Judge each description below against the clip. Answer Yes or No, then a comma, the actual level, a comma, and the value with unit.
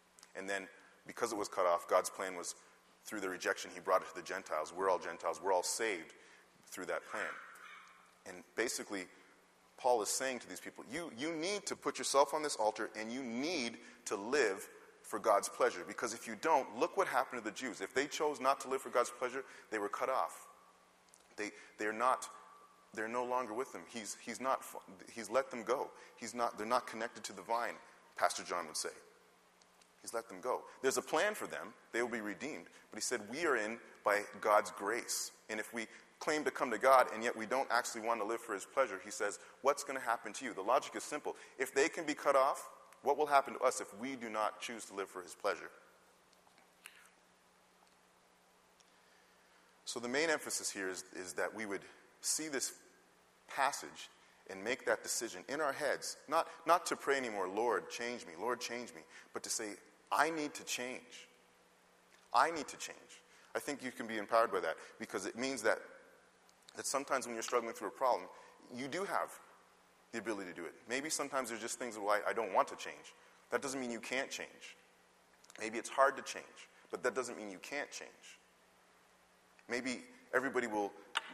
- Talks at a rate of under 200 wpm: No, fast, 205 wpm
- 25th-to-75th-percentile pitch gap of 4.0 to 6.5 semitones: Yes, average, 4.8 semitones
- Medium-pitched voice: No, low, 120 Hz